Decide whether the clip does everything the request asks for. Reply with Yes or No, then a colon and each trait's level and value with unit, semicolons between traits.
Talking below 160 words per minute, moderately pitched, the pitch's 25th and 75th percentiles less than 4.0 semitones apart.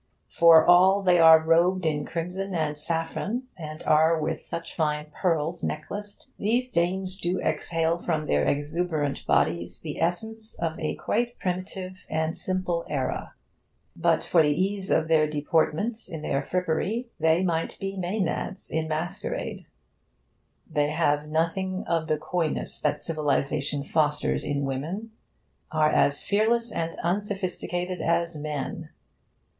Yes: slow, 135 wpm; medium, 165 Hz; average, 3.3 semitones